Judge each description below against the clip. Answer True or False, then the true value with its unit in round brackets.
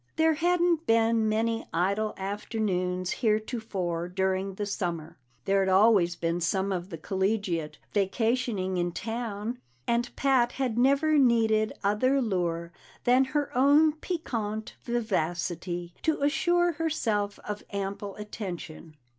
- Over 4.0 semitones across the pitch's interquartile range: True (4.8 semitones)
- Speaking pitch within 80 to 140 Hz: False (215 Hz)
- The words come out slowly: True (120 wpm)